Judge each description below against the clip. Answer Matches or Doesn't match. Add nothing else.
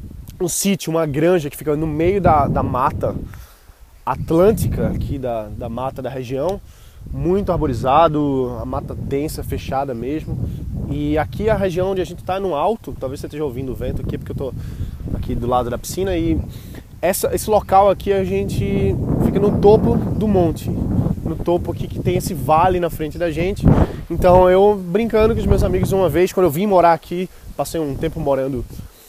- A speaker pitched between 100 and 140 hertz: Doesn't match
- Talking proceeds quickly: Matches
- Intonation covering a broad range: Matches